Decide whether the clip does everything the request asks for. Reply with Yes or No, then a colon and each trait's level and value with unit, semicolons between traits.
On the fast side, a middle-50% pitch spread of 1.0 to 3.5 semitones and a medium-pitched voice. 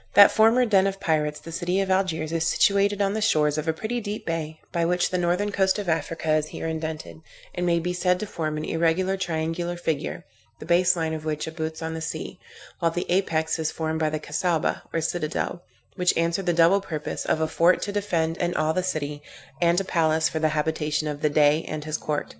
Yes: fast, 225 wpm; narrow, 2.5 semitones; medium, 165 Hz